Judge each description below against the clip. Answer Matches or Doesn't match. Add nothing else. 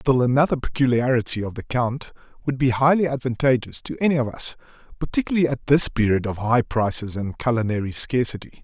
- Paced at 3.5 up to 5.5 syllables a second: Doesn't match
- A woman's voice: Doesn't match